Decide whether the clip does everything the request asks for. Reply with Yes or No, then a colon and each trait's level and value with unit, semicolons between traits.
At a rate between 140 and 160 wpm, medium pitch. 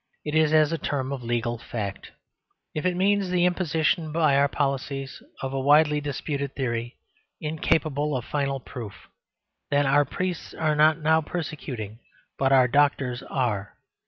Yes: average, 155 wpm; medium, 145 Hz